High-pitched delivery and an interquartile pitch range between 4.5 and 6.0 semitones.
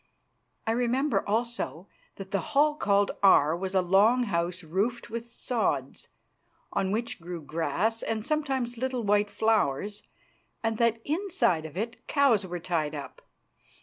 Yes: high, 210 Hz; average, 5.1 semitones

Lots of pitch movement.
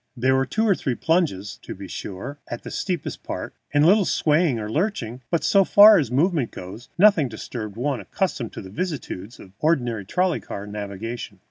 Yes: wide, 8.2 semitones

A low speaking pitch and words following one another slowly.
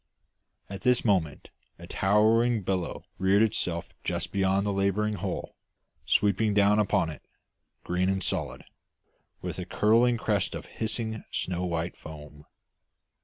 Yes: low, 100 Hz; slow, 130 wpm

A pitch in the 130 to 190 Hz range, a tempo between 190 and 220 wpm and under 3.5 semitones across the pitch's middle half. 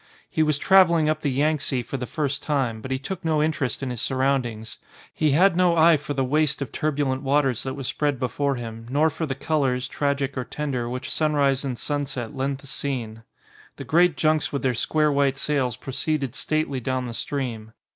Yes: medium, 140 Hz; average, 200 wpm; average, 2.8 semitones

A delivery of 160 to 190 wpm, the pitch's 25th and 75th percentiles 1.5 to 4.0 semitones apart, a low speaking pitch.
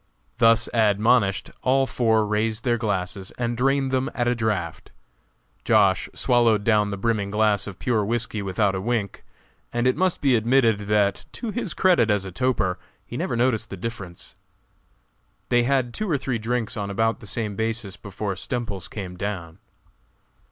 Yes: average, 165 wpm; average, 3.2 semitones; low, 110 Hz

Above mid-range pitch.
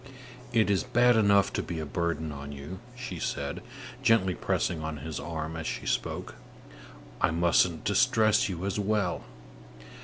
No: very low, 90 Hz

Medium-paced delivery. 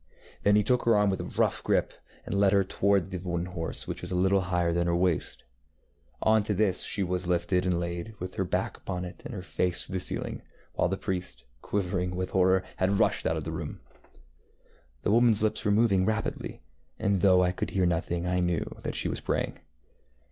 No: fast, 215 wpm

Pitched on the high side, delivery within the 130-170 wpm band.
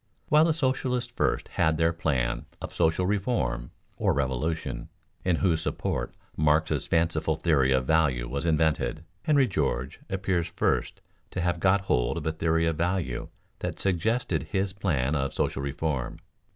No: very low, 80 Hz; average, 150 wpm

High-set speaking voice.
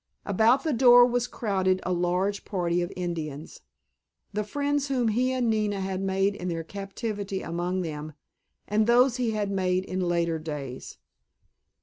Yes: high, 195 Hz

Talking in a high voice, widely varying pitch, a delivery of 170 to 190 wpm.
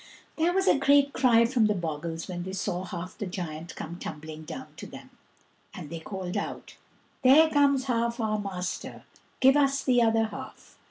Yes: high, 215 Hz; wide, 7.0 semitones; average, 180 wpm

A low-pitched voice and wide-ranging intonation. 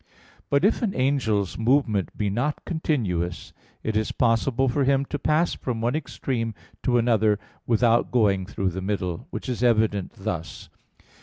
No: low, 115 Hz; average, 4.7 semitones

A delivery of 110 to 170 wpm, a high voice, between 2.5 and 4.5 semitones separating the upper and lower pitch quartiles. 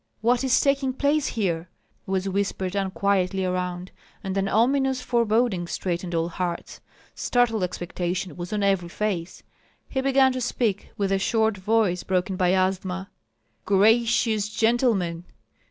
Yes: slow, 135 wpm; high, 195 Hz; average, 4.1 semitones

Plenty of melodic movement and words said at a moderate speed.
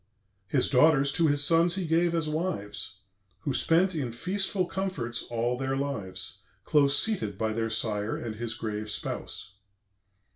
Yes: wide, 6.8 semitones; average, 150 wpm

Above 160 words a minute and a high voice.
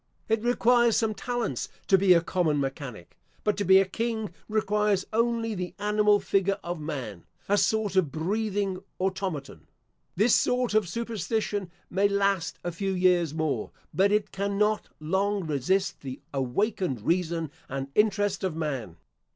No: average, 150 wpm; high, 195 Hz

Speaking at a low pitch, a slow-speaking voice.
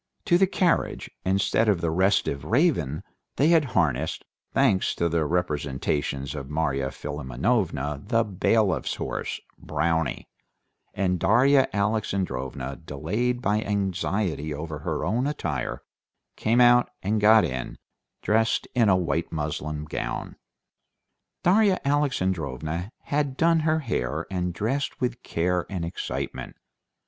Yes: very low, 95 Hz; slow, 120 wpm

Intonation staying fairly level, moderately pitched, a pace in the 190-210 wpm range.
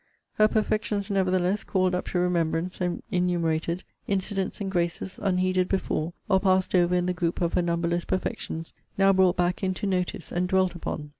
No: narrow, 1.6 semitones; medium, 180 Hz; average, 170 wpm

